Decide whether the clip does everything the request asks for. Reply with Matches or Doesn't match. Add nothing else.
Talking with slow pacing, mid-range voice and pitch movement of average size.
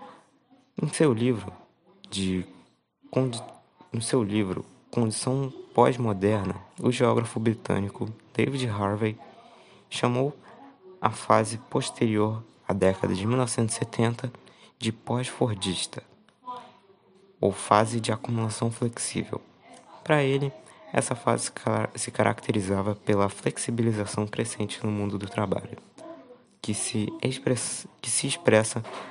Doesn't match